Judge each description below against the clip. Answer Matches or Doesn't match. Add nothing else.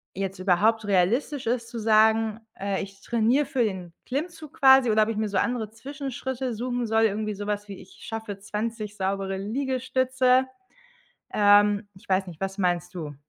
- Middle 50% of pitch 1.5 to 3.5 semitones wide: Doesn't match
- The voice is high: Matches